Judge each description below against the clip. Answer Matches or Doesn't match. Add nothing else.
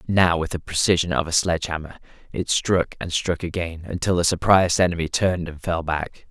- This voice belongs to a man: Matches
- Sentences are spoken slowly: Doesn't match